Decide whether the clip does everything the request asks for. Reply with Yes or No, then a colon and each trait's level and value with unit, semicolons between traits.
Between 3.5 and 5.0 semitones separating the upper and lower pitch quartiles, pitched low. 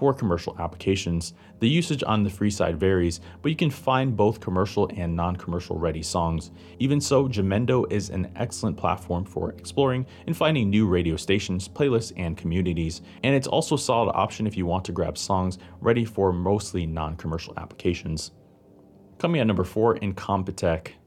Yes: average, 4.6 semitones; very low, 95 Hz